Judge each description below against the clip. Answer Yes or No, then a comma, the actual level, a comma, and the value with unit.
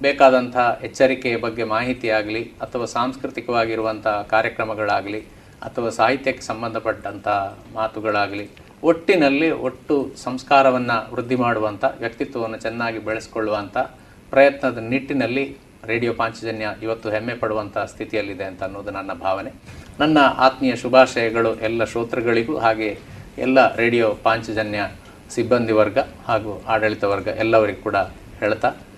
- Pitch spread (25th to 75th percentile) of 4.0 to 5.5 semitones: No, average, 2.9 semitones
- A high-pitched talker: No, low, 115 Hz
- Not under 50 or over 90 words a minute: No, average, 100 wpm